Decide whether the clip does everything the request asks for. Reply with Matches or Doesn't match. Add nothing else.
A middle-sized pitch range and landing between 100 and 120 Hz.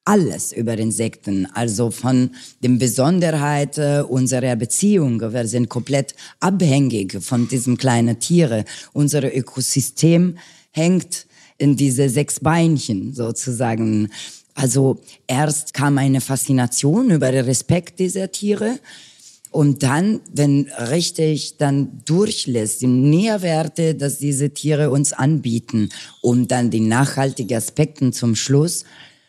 Doesn't match